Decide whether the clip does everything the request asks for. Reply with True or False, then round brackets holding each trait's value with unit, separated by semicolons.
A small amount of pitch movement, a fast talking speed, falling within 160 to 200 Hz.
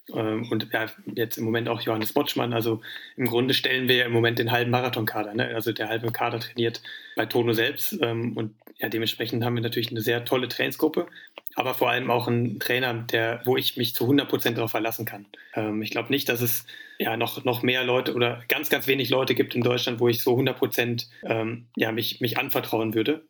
False (1.5 semitones; 215 wpm; 120 Hz)